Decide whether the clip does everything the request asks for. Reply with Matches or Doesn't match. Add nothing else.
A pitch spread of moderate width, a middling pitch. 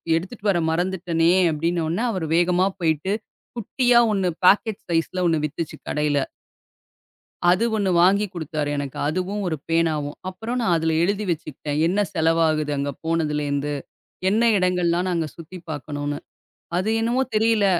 Matches